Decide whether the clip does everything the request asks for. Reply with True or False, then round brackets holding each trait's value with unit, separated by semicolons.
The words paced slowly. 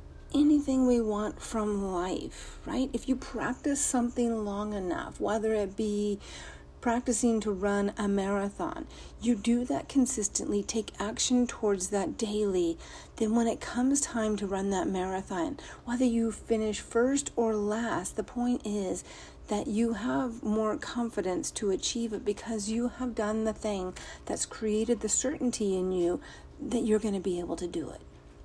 False (160 wpm)